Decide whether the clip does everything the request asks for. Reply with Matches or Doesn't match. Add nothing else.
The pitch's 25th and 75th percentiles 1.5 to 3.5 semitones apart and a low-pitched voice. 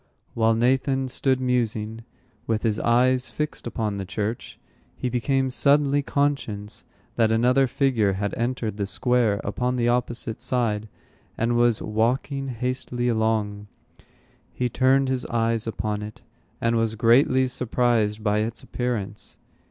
Matches